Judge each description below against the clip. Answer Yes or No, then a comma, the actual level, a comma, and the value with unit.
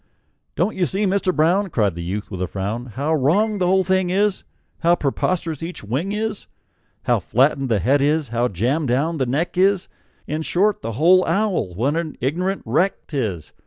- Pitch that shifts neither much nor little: No, wide, 7.3 semitones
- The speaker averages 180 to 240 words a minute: Yes, average, 195 wpm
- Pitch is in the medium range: Yes, medium, 155 Hz